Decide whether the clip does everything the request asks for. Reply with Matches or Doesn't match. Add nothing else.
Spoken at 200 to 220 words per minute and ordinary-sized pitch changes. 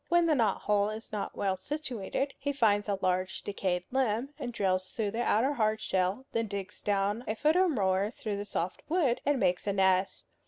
Matches